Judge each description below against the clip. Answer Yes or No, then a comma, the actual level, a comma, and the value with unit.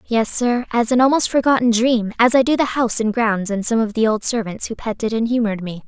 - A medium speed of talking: No, fast, 255 wpm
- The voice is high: Yes, high, 230 Hz